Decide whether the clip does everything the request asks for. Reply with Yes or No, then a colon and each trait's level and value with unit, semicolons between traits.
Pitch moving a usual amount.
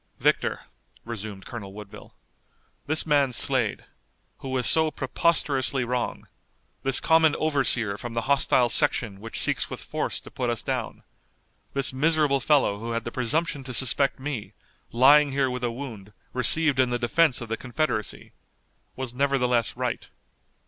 Yes: average, 3.2 semitones